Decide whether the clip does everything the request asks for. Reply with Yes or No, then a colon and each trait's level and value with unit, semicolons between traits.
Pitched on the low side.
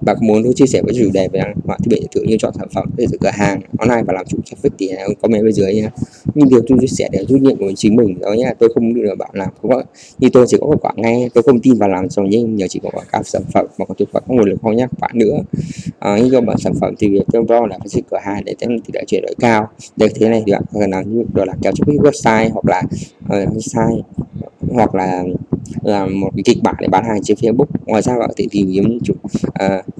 Yes: low, 110 Hz